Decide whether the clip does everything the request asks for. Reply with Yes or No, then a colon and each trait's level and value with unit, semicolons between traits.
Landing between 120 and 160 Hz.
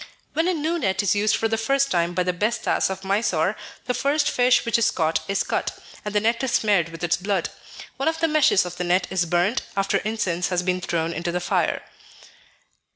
No: high, 195 Hz